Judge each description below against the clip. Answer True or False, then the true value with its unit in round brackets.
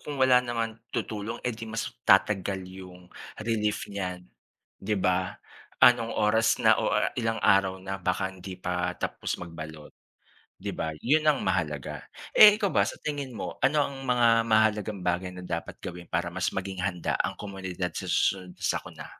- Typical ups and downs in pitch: True (4.0 semitones)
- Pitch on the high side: False (95 Hz)